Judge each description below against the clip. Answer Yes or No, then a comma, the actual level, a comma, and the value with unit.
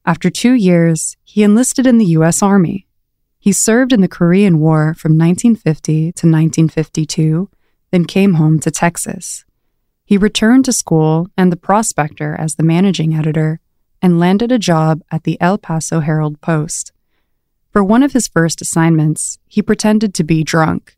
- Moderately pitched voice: Yes, medium, 170 Hz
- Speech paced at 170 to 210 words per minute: No, average, 160 wpm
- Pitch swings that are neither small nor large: Yes, average, 4.2 semitones